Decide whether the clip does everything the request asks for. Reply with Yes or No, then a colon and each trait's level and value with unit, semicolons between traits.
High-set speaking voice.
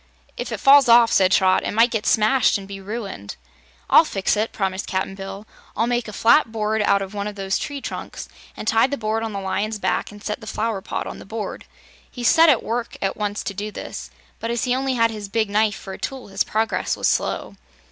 Yes: high, 215 Hz